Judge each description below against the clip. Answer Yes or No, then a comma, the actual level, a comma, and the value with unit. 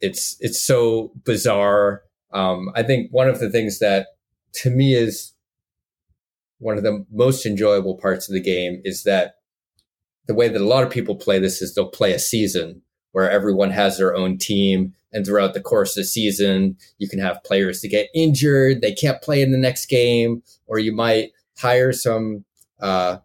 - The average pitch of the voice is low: Yes, low, 105 Hz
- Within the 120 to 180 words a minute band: No, average, 190 wpm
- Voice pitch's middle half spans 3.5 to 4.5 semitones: Yes, average, 3.8 semitones